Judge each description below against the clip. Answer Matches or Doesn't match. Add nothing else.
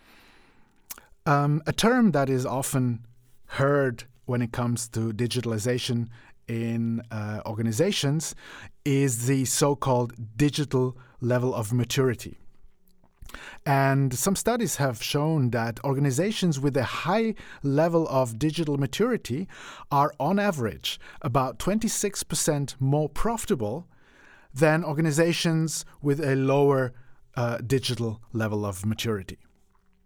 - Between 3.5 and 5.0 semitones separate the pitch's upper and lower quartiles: Matches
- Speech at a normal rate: Doesn't match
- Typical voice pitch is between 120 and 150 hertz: Matches